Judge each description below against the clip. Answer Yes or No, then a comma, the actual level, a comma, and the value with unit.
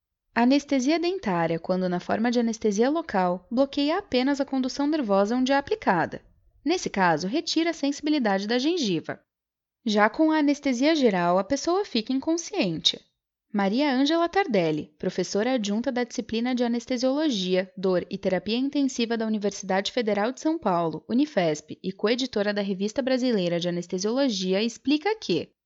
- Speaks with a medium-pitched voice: No, high, 240 Hz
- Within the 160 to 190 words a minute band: No, average, 145 wpm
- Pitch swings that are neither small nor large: No, wide, 6.3 semitones